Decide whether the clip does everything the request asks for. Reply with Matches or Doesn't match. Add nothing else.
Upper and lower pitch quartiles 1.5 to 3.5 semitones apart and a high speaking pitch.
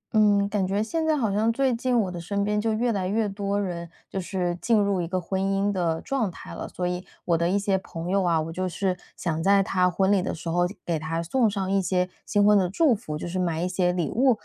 Matches